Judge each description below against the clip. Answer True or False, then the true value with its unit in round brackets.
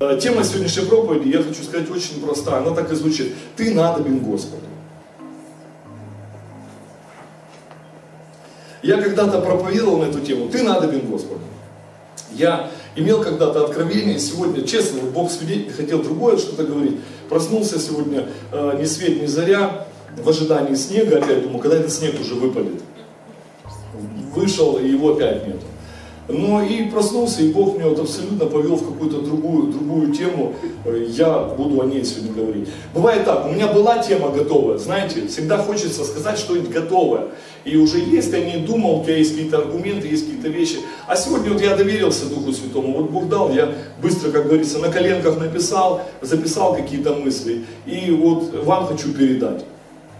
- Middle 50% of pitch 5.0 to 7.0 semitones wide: True (5.4 semitones)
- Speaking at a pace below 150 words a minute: False (155 wpm)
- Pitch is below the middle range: False (160 Hz)